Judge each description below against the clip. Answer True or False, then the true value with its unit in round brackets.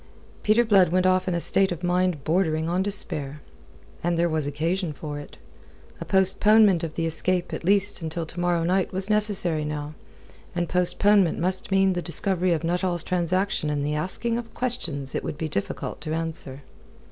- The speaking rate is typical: True (180 wpm)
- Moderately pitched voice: True (175 Hz)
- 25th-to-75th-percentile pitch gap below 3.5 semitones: True (3.1 semitones)